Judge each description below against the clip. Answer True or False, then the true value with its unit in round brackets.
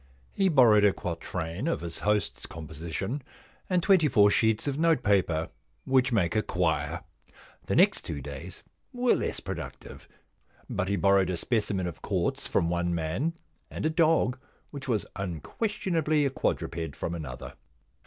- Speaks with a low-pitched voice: True (100 Hz)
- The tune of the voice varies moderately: False (8.9 semitones)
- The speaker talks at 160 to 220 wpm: False (150 wpm)